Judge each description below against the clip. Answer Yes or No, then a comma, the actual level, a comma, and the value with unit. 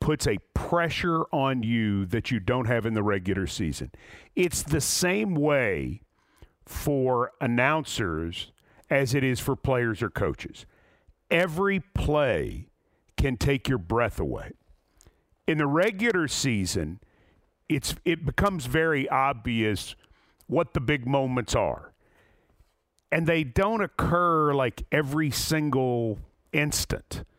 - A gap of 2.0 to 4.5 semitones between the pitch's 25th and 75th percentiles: No, wide, 5.4 semitones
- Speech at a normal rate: No, slow, 120 wpm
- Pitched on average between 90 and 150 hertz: Yes, low, 135 Hz